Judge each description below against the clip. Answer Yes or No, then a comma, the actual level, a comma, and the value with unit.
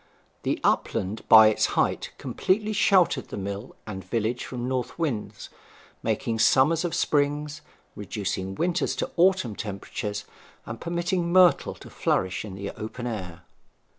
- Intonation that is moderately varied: No, wide, 8.4 semitones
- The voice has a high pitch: No, low, 120 Hz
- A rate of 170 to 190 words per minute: No, slow, 135 wpm